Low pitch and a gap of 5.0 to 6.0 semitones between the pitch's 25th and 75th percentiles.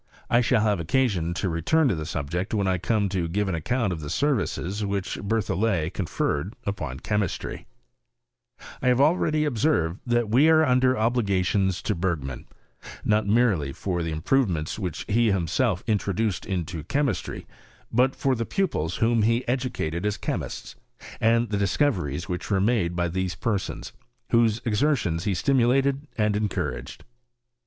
Yes: low, 105 Hz; wide, 5.4 semitones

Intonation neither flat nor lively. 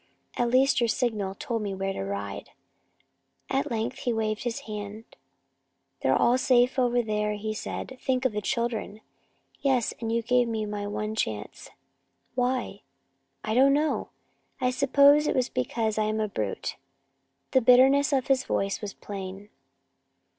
Yes: average, 3.4 semitones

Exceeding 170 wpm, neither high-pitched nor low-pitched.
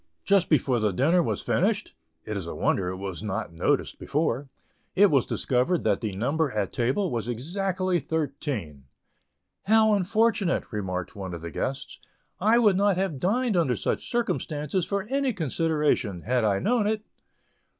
No: average, 165 wpm; medium, 150 Hz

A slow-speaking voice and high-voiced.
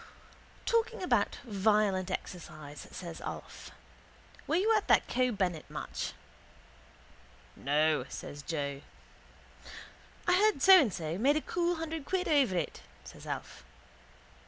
Yes: slow, 125 wpm; high, 215 Hz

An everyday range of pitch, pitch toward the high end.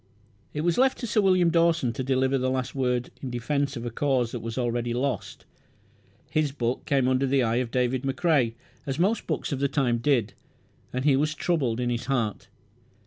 No: average, 3.2 semitones; low, 130 Hz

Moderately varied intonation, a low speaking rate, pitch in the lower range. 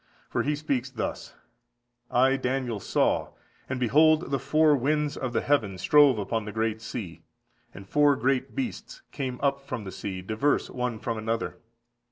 No: average, 4.4 semitones; average, 165 wpm; low, 130 Hz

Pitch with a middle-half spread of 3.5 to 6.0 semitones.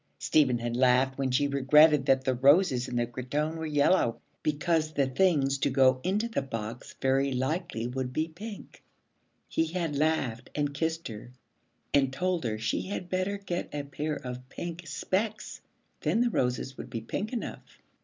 Yes: average, 4.5 semitones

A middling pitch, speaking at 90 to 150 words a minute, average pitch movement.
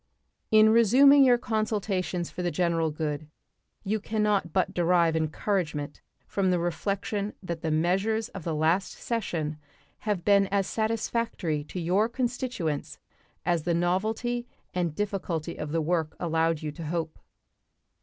Yes: medium, 180 Hz; average, 145 wpm; average, 4.7 semitones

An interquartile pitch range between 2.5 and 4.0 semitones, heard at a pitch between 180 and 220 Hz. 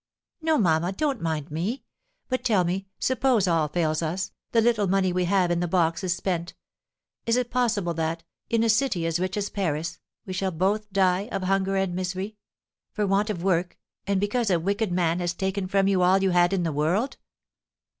Yes: average, 3.0 semitones; high, 190 Hz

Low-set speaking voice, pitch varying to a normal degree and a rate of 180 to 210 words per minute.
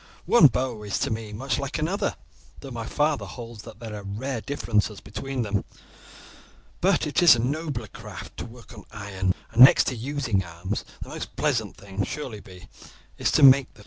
Yes: low, 115 Hz; average, 4.7 semitones; average, 185 wpm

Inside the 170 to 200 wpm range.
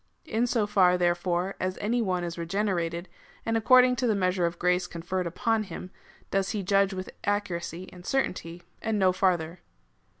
Yes: average, 175 wpm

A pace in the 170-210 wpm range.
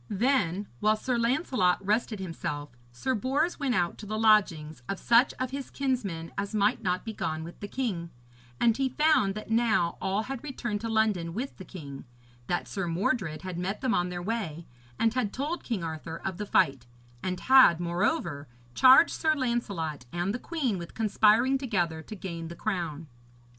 Yes: average, 185 wpm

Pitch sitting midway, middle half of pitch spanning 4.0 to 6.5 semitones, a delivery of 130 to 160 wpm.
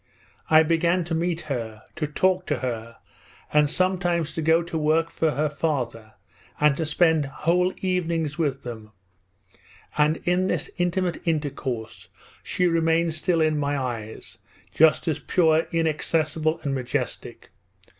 No: medium, 160 Hz; average, 2.8 semitones; average, 140 wpm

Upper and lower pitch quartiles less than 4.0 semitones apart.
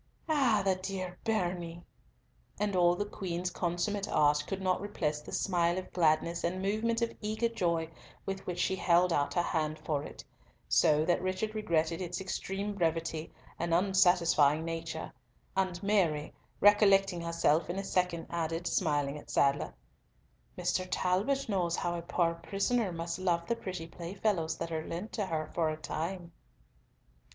Yes: average, 2.8 semitones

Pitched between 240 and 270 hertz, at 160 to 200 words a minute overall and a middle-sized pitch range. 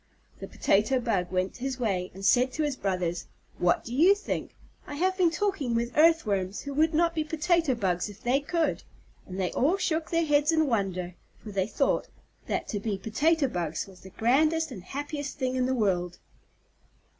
No: very high, 255 Hz; average, 190 wpm; wide, 8.2 semitones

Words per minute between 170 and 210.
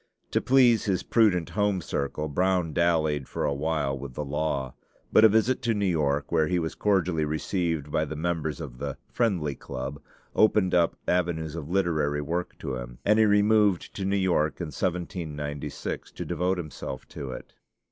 Yes: average, 180 wpm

